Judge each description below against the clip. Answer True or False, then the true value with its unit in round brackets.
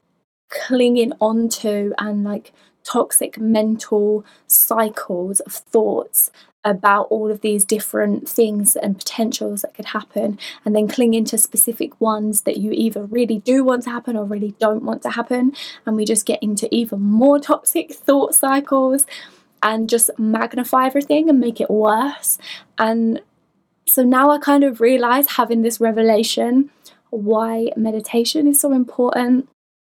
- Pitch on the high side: True (230 Hz)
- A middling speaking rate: True (145 wpm)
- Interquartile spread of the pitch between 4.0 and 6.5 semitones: False (3.2 semitones)